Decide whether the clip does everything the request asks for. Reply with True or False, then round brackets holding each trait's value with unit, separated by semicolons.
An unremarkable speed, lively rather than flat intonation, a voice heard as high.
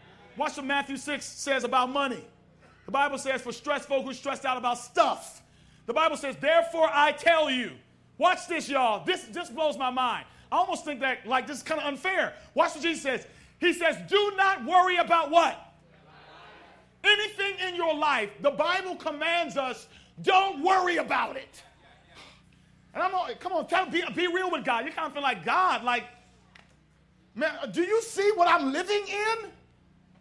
False (185 wpm; 4.7 semitones; 315 Hz)